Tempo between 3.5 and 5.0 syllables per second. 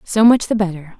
No: 5.6 syllables/s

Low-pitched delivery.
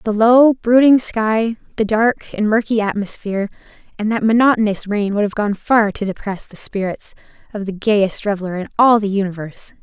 No: high, 210 Hz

